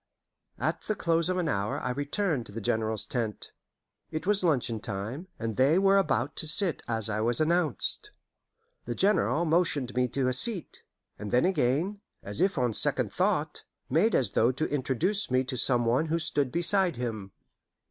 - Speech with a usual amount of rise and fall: No, wide, 6.5 semitones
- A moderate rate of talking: Yes, average, 180 wpm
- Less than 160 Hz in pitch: Yes, medium, 140 Hz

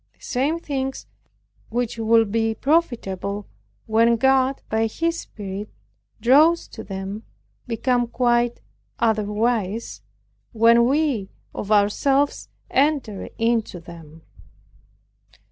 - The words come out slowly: Yes, slow, 95 wpm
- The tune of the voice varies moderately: Yes, average, 4.0 semitones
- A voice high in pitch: Yes, high, 230 Hz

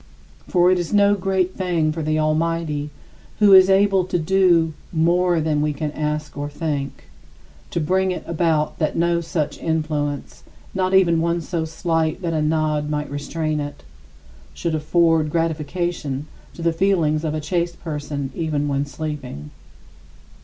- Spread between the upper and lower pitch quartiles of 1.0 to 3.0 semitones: Yes, narrow, 2.5 semitones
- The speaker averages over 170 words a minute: No, average, 155 wpm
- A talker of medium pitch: Yes, medium, 160 Hz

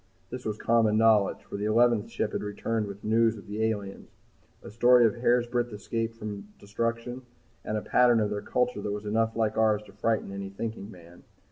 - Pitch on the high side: No, low, 110 Hz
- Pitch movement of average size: No, narrow, 2.0 semitones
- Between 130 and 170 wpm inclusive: No, fast, 205 wpm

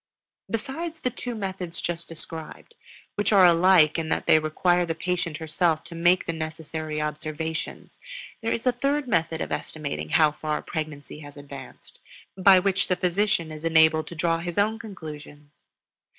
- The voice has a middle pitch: Yes, medium, 165 Hz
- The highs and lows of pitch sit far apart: No, average, 3.4 semitones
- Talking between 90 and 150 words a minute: No, average, 165 wpm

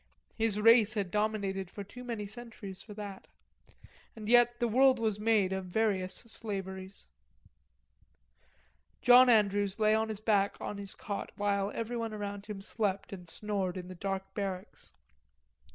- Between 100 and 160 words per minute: Yes, average, 150 wpm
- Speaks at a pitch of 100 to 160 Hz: No, high, 205 Hz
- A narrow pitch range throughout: Yes, narrow, 2.3 semitones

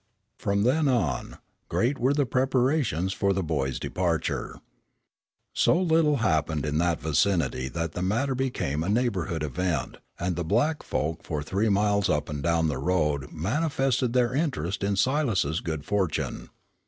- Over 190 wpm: No, average, 155 wpm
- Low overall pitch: Yes, very low, 95 Hz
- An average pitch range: No, wide, 8.1 semitones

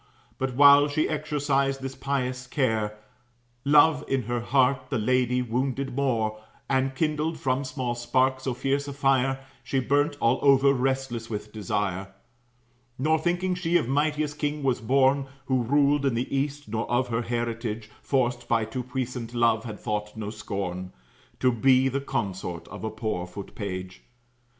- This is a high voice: No, low, 130 Hz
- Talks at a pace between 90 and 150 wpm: No, average, 160 wpm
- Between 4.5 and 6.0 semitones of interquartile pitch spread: No, average, 3.4 semitones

